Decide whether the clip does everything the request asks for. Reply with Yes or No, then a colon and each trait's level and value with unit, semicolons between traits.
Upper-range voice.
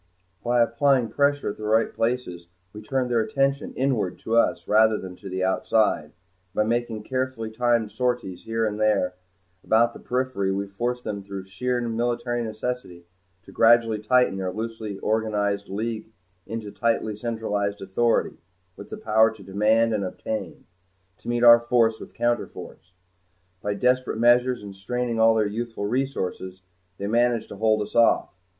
No: low, 110 Hz